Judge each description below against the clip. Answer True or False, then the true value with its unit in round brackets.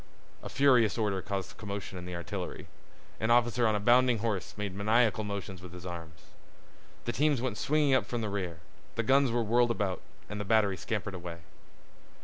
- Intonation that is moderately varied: True (4.0 semitones)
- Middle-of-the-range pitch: False (105 Hz)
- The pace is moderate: True (185 wpm)